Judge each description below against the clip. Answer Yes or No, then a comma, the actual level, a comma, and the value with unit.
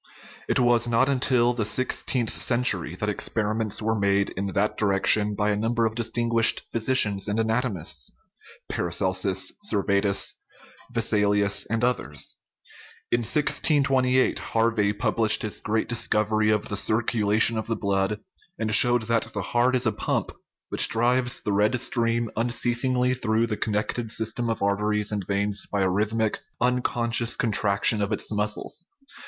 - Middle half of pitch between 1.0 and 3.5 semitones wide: Yes, narrow, 2.6 semitones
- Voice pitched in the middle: No, low, 110 Hz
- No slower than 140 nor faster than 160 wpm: Yes, average, 150 wpm